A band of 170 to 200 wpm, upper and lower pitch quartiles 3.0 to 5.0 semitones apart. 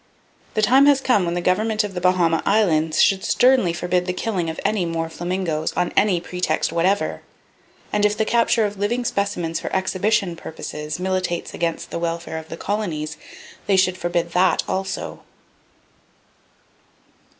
No: average, 160 wpm; average, 3.5 semitones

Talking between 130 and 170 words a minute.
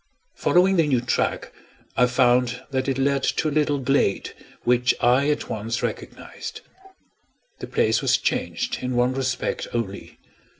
Yes: average, 145 wpm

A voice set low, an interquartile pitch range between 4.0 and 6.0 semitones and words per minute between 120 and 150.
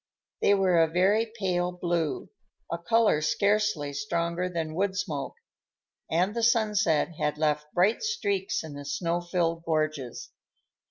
No: medium, 175 Hz; average, 4.3 semitones; average, 140 wpm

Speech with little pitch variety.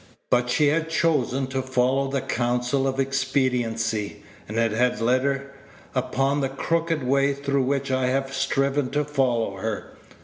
Yes: narrow, 2.0 semitones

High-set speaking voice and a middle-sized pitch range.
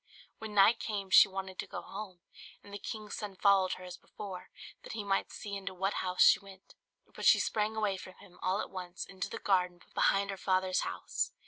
No: high, 195 Hz; narrow, 1.7 semitones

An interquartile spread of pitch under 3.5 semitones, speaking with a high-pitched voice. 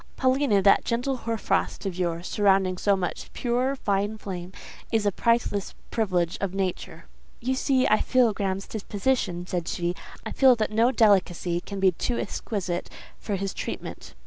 No: average, 4.0 semitones; high, 200 Hz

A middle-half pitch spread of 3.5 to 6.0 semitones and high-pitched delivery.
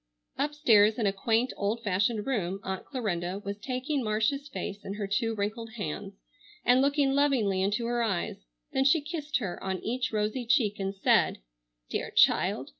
Yes: average, 4.5 semitones; high, 220 Hz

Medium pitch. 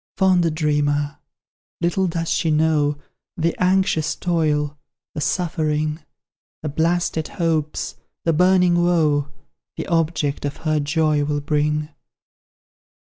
Yes: medium, 155 Hz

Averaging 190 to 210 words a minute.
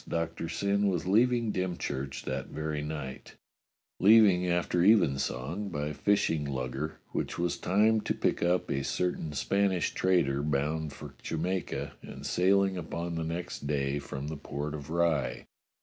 No: average, 150 wpm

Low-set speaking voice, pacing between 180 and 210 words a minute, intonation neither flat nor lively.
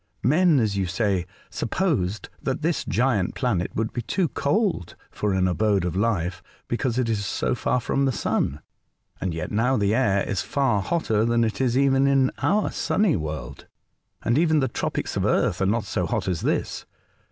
No: low, 115 Hz; average, 190 wpm; wide, 5.8 semitones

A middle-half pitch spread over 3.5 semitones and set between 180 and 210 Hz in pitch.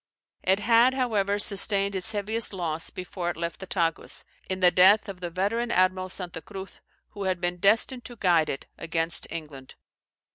No: average, 2.9 semitones; high, 190 Hz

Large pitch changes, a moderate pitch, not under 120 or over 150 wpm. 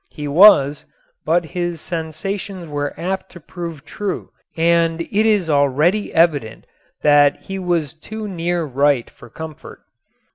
No: average, 3.6 semitones; medium, 165 Hz; slow, 135 wpm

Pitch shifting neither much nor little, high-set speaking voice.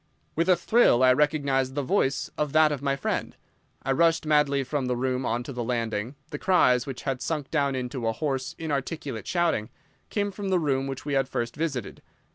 No: average, 3.3 semitones; low, 135 Hz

